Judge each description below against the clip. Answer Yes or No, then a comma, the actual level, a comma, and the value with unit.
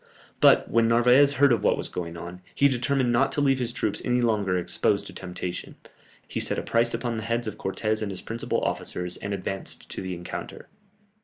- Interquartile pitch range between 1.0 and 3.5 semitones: No, average, 4.4 semitones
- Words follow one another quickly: Yes, fast, 210 wpm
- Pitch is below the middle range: Yes, low, 115 Hz